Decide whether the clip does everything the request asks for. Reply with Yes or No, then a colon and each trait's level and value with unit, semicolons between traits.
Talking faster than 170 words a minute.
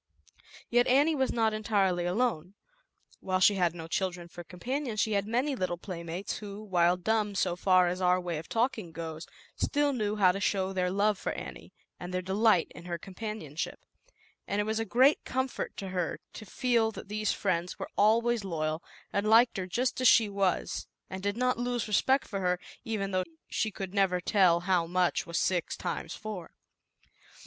Yes: average, 190 wpm